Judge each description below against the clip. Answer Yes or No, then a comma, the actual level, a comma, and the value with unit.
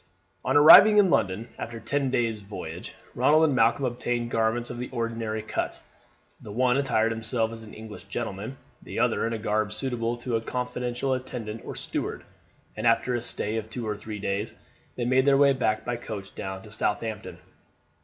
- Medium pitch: No, low, 115 Hz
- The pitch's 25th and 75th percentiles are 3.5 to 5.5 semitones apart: No, narrow, 2.5 semitones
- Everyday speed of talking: Yes, average, 185 wpm